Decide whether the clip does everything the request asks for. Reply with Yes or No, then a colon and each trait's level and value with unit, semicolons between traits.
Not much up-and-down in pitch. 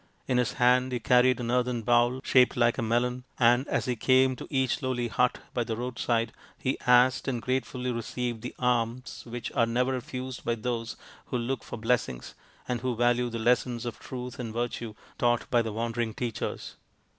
Yes: narrow, 1.3 semitones